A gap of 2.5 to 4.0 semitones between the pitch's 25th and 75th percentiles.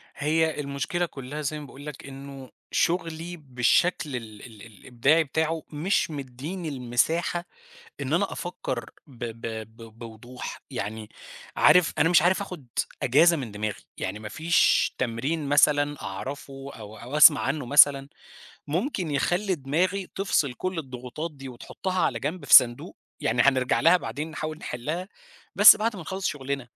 No: average, 4.8 semitones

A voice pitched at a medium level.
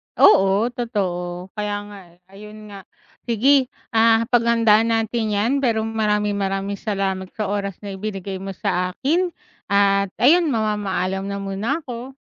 No: high, 210 Hz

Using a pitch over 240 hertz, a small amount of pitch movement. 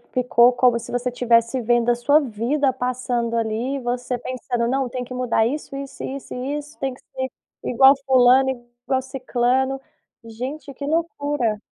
Yes: very high, 255 Hz; narrow, 2.0 semitones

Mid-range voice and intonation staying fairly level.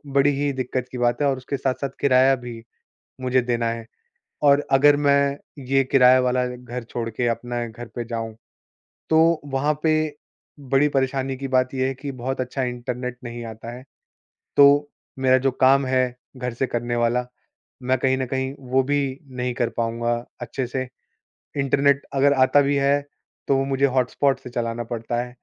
No: low, 130 Hz; narrow, 2.1 semitones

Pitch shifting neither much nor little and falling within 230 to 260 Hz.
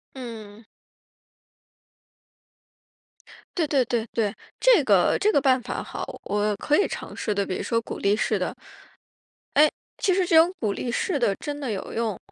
No: wide, 6.0 semitones; high, 240 Hz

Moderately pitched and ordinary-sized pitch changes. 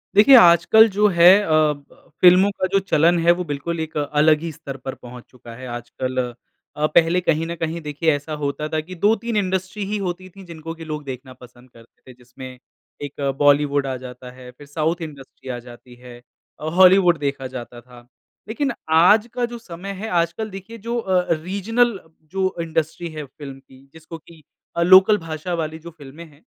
Yes: medium, 160 Hz; average, 5.0 semitones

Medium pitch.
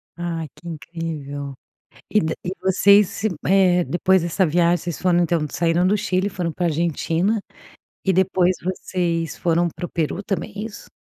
Yes: medium, 175 Hz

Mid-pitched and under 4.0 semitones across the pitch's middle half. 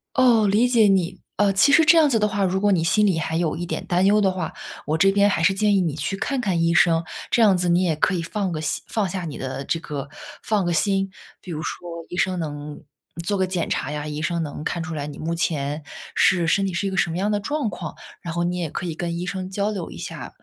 Yes: medium, 180 Hz; average, 3.5 semitones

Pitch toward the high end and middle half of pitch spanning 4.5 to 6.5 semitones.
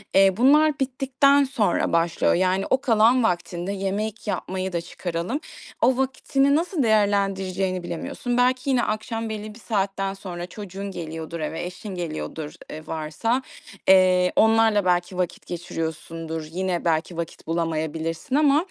Yes: high, 195 Hz; average, 5.1 semitones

